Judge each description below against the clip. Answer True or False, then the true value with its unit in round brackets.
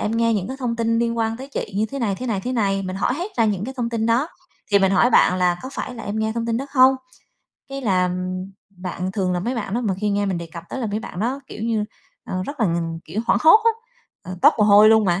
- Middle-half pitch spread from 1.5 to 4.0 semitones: True (3.7 semitones)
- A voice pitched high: True (220 Hz)